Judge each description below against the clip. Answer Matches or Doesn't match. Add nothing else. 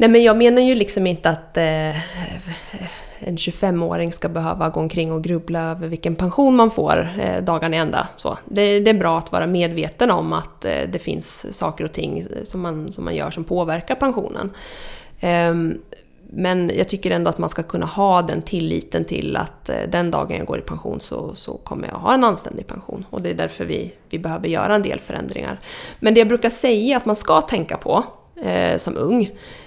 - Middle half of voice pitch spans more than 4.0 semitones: Matches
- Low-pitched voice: Doesn't match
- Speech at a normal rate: Doesn't match